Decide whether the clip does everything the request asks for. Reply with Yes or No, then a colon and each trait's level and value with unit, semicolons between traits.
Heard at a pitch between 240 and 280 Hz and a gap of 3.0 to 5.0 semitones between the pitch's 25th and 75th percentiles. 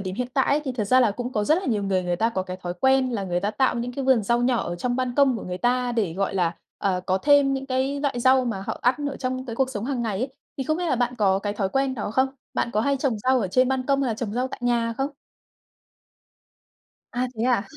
Yes: high, 245 Hz; average, 4.3 semitones